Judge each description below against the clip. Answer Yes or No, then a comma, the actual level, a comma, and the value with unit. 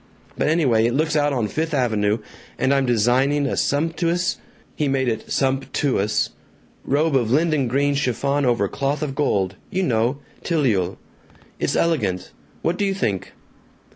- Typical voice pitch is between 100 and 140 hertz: Yes, low, 135 Hz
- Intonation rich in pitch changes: No, average, 4.5 semitones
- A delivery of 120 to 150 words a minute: No, average, 165 wpm